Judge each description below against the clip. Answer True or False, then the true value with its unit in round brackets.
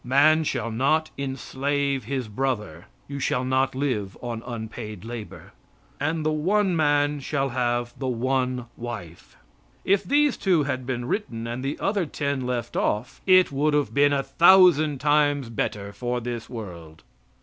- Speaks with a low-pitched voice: True (130 Hz)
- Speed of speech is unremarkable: True (155 wpm)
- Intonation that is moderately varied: True (3.6 semitones)